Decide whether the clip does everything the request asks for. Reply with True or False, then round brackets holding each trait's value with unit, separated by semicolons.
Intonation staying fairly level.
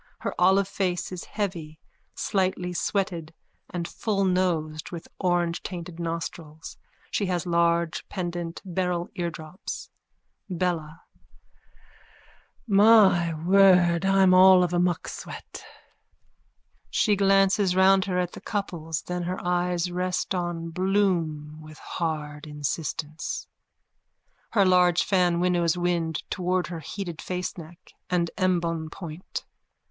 True (1.9 semitones)